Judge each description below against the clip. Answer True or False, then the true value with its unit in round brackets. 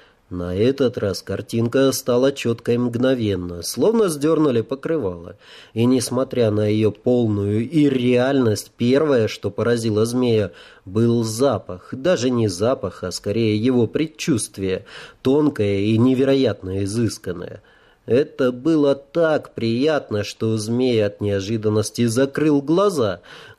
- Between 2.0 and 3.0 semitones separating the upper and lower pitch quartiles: False (4.1 semitones)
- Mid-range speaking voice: False (120 Hz)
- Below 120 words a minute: True (110 wpm)